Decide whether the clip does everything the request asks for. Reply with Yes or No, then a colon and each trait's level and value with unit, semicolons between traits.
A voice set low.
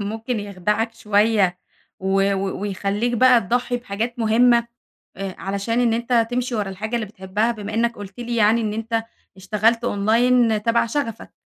No: high, 220 Hz